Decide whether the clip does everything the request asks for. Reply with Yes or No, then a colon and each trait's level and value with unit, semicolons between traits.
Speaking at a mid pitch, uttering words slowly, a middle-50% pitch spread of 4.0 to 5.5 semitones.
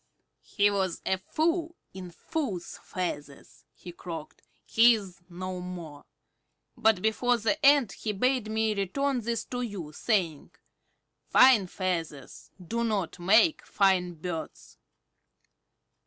No: high, 195 Hz; slow, 120 wpm; average, 4.8 semitones